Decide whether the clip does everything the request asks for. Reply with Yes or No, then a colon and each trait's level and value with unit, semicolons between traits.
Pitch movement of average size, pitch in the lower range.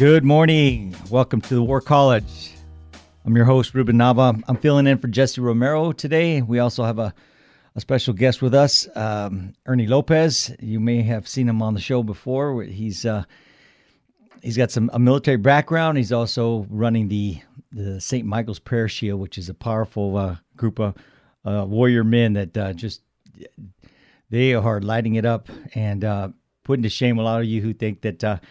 Yes: average, 3.4 semitones; low, 115 Hz